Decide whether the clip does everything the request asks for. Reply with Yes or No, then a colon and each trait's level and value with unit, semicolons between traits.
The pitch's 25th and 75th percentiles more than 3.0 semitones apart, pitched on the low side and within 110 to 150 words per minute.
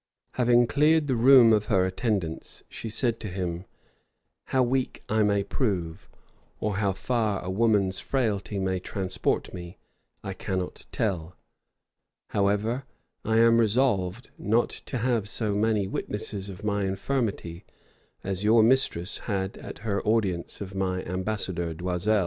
Yes: average, 3.5 semitones; low, 105 Hz; average, 140 wpm